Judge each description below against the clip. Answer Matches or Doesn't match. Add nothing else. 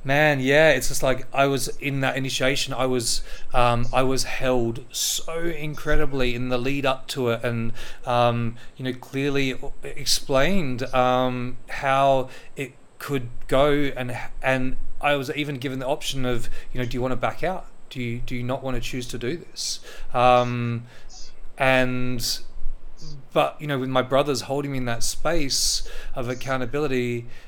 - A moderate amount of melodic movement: Doesn't match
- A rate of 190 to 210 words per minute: Doesn't match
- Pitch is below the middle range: Matches